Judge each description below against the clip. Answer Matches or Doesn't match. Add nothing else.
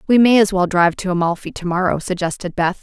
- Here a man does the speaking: Doesn't match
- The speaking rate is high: Matches